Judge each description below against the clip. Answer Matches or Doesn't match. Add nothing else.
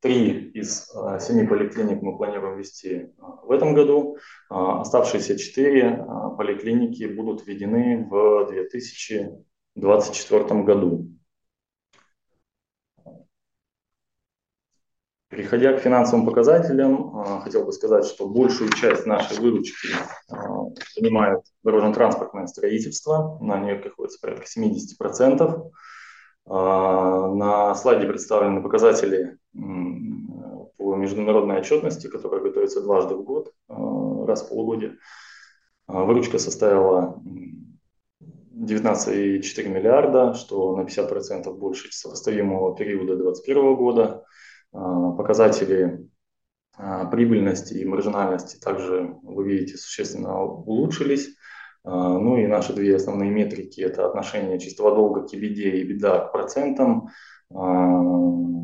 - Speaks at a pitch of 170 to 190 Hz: Doesn't match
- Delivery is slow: Matches